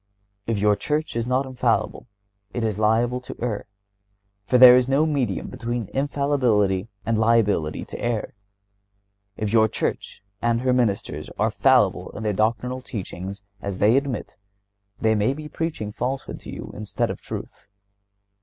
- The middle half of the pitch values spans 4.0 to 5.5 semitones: No, average, 3.3 semitones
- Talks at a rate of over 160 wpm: No, average, 155 wpm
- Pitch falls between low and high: No, low, 115 Hz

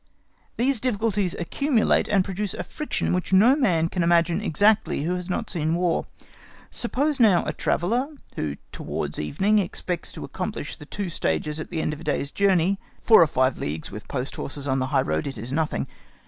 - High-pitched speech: No, medium, 175 Hz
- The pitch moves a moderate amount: No, wide, 5.9 semitones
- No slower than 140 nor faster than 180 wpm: No, average, 190 wpm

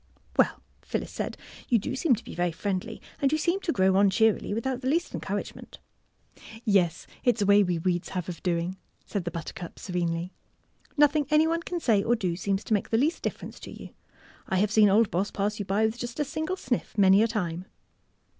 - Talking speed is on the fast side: Yes, fast, 230 wpm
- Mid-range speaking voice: No, high, 205 Hz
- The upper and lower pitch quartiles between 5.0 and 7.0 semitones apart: Yes, wide, 5.4 semitones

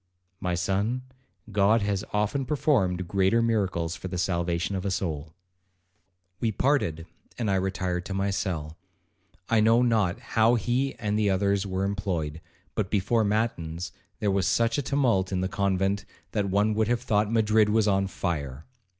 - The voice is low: Yes, low, 100 Hz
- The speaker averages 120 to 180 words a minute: Yes, average, 165 wpm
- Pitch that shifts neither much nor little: Yes, average, 3.1 semitones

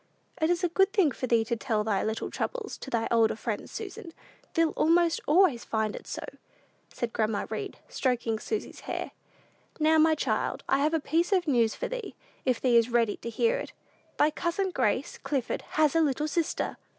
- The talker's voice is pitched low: No, very high, 295 Hz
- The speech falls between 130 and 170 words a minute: No, average, 195 wpm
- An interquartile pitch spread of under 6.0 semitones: No, wide, 6.7 semitones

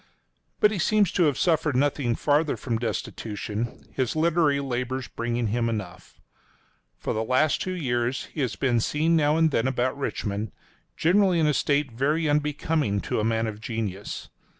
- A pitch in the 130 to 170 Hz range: Yes, low, 135 Hz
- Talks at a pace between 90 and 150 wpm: No, average, 170 wpm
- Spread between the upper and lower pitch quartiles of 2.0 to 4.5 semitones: No, average, 5.2 semitones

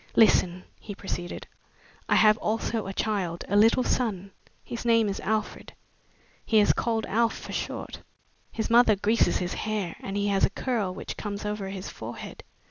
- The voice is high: Yes, high, 210 Hz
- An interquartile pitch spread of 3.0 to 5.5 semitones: No, narrow, 2.4 semitones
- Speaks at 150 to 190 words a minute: Yes, average, 170 wpm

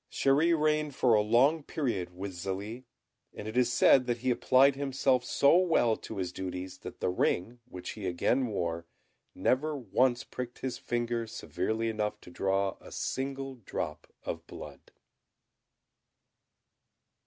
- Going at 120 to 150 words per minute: Yes, average, 145 wpm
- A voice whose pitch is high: No, low, 120 Hz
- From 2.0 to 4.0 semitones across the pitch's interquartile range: No, wide, 5.4 semitones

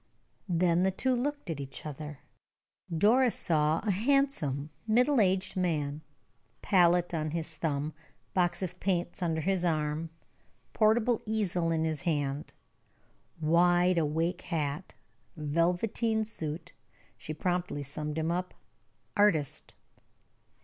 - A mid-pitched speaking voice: Yes, medium, 170 Hz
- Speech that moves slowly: Yes, slow, 115 wpm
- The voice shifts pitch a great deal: No, average, 3.8 semitones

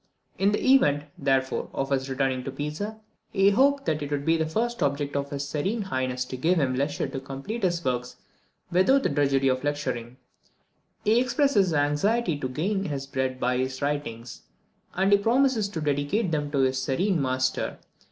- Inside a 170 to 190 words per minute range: Yes, average, 185 wpm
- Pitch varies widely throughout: Yes, wide, 6.7 semitones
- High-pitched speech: No, medium, 145 Hz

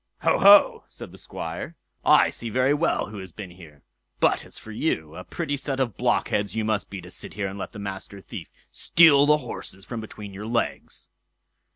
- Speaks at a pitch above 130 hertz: No, low, 105 Hz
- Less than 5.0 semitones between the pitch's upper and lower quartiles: No, wide, 5.5 semitones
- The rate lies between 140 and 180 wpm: No, fast, 205 wpm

